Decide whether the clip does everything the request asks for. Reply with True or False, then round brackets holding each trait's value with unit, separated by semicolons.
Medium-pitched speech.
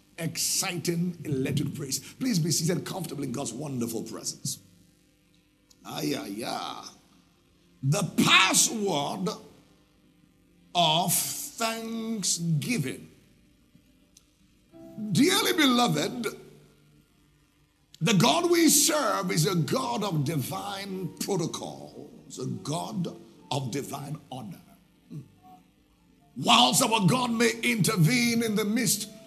True (175 Hz)